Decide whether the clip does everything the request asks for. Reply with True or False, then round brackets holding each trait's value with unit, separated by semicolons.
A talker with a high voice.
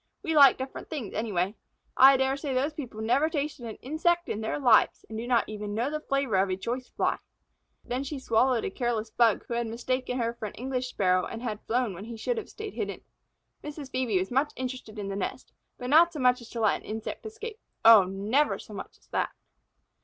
True (250 Hz)